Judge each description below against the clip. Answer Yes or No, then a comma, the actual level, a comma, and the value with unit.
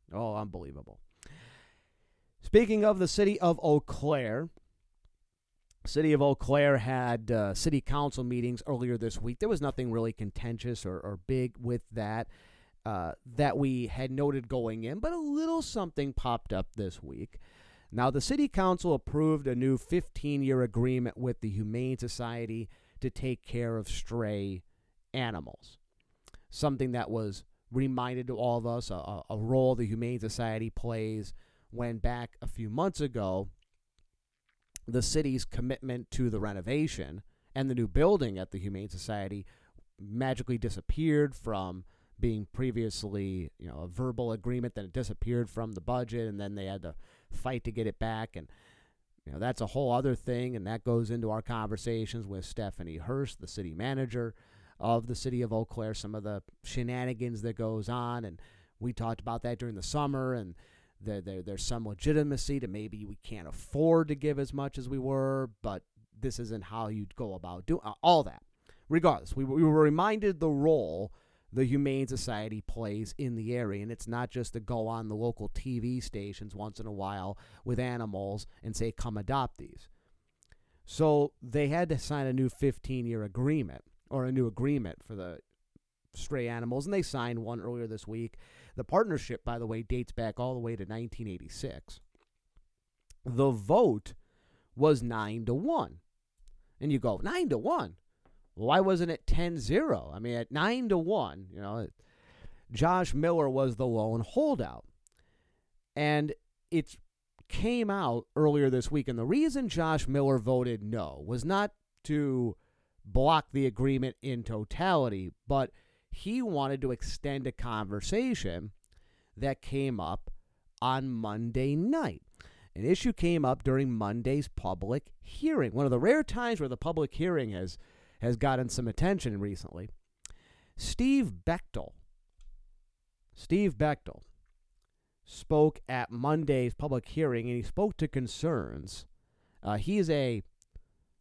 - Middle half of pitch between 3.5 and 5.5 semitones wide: Yes, average, 4.5 semitones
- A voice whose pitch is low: Yes, low, 120 Hz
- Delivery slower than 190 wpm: Yes, average, 160 wpm